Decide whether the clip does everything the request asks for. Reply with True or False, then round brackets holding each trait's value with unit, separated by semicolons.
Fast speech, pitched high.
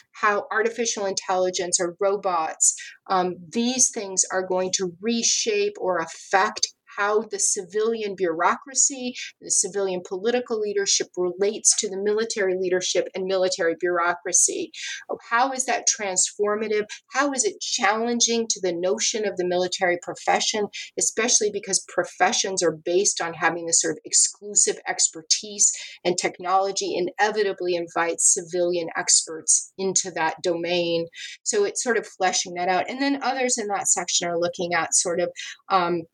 False (140 wpm; 195 Hz)